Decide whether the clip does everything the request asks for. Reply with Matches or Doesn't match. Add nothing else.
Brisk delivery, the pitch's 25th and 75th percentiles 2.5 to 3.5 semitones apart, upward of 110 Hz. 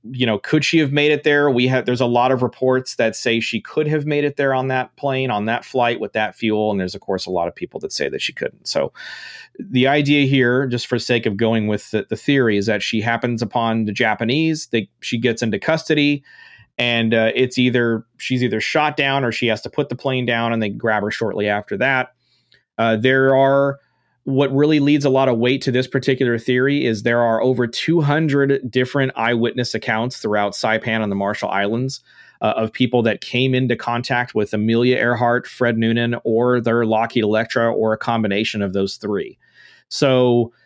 Matches